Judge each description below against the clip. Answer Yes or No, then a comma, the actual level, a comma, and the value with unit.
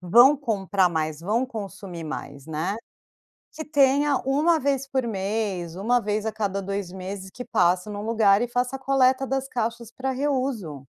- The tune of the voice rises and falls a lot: Yes, wide, 5.7 semitones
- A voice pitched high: Yes, high, 220 Hz